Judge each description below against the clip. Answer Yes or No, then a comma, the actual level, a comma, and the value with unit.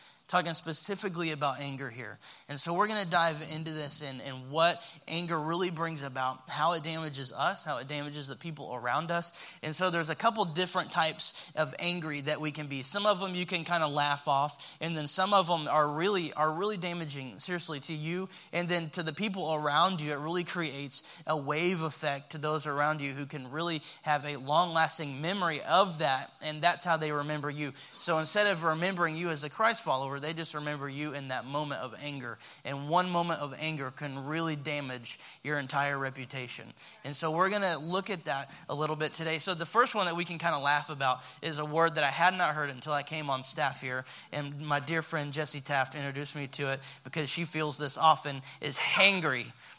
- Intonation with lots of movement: No, average, 3.1 semitones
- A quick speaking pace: Yes, fast, 220 wpm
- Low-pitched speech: No, medium, 155 Hz